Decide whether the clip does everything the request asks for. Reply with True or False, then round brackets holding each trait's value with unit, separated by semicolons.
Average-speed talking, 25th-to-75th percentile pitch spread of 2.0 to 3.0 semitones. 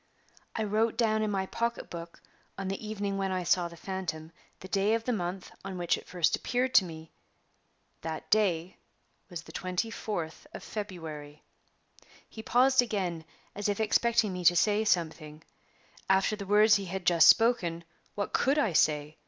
False (170 wpm; 4.2 semitones)